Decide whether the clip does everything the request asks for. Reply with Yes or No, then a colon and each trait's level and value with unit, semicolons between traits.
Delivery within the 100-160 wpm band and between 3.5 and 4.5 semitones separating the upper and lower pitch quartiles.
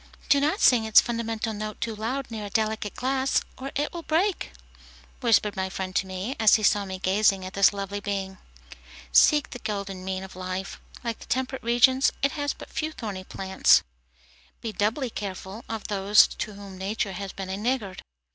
No: average, 190 wpm; average, 4.2 semitones